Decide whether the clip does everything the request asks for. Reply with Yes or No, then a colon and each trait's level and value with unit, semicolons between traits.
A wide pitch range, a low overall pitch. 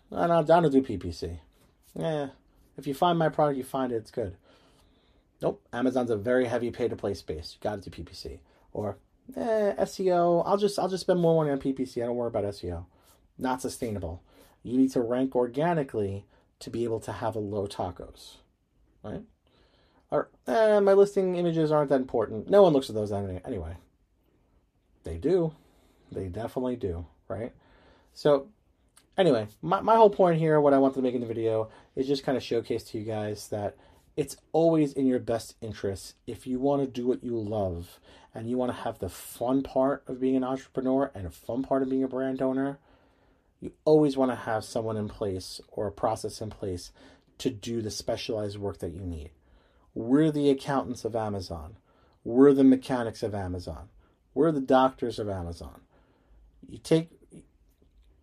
Yes: wide, 5.7 semitones; low, 120 Hz